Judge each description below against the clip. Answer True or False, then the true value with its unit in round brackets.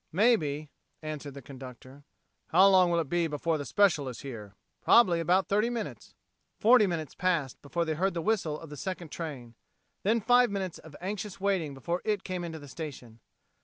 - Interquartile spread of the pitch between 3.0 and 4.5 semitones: False (5.1 semitones)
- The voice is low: False (170 Hz)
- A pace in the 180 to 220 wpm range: True (185 wpm)